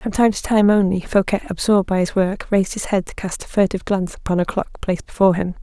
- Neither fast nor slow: No, fast, 255 wpm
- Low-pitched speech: No, high, 195 Hz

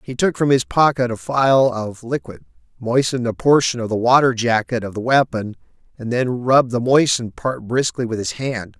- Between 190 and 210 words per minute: Yes, average, 200 wpm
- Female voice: No, male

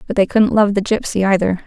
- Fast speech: Yes, fast, 250 wpm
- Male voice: No, female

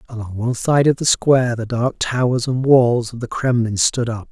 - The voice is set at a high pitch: No, low, 120 Hz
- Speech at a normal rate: No, fast, 220 wpm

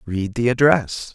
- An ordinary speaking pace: Yes, average, 155 wpm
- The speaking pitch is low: Yes, low, 115 Hz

